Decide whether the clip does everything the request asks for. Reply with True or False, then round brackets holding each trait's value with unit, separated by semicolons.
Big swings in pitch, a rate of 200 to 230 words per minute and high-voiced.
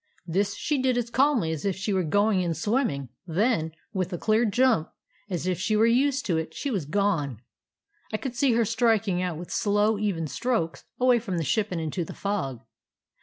True (5.7 semitones; 205 wpm; 200 Hz)